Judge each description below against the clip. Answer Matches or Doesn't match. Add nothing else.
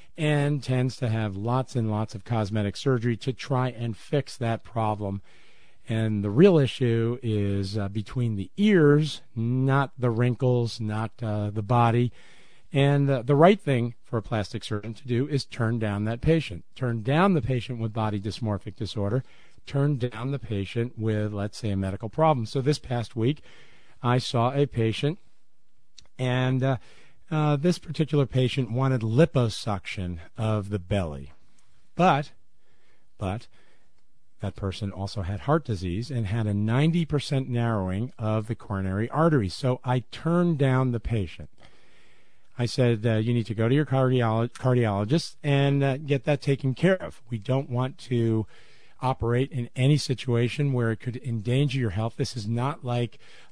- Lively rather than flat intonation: Doesn't match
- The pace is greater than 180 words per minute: Doesn't match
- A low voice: Matches